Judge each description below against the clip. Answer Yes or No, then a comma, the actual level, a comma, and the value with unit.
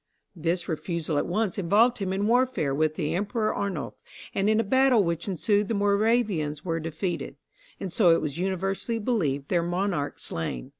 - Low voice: No, medium, 185 Hz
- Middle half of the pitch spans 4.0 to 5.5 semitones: Yes, average, 4.4 semitones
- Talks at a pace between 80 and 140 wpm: No, average, 170 wpm